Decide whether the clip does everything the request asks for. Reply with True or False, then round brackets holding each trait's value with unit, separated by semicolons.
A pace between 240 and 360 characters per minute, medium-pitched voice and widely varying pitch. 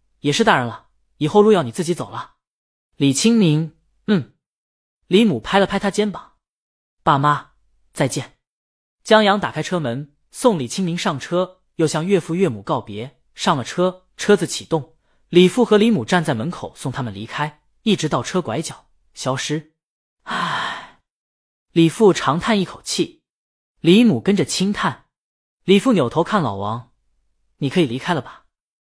False (225 characters per minute; 165 Hz; 5.8 semitones)